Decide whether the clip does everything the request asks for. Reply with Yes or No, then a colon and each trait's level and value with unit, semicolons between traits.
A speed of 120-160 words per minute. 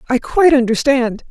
Yes: average, 140 wpm